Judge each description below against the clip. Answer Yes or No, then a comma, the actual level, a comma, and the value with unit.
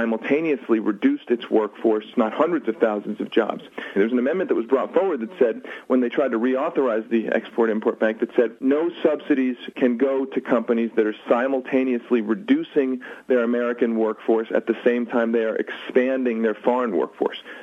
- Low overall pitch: Yes, low, 120 Hz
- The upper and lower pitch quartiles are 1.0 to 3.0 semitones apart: Yes, narrow, 2.5 semitones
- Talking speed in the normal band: Yes, average, 175 wpm